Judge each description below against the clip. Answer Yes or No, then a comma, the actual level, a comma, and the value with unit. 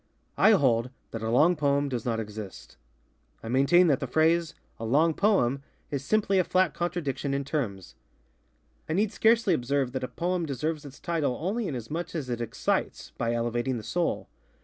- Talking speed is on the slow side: No, average, 175 wpm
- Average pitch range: No, wide, 6.0 semitones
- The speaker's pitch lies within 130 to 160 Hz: Yes, medium, 140 Hz